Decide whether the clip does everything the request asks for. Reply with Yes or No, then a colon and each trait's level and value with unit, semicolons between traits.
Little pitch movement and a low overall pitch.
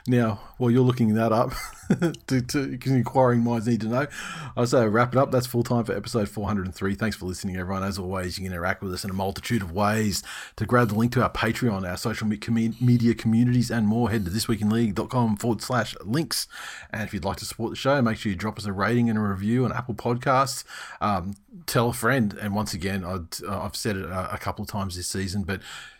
No: average, 3.3 semitones; low, 110 Hz